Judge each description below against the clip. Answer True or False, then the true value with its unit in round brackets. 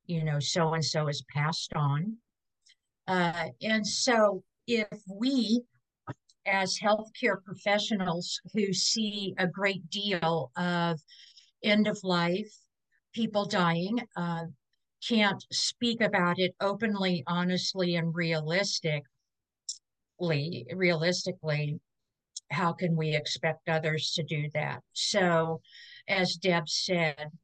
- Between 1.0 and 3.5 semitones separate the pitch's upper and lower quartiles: False (3.9 semitones)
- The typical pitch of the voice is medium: True (175 Hz)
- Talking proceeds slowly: True (105 wpm)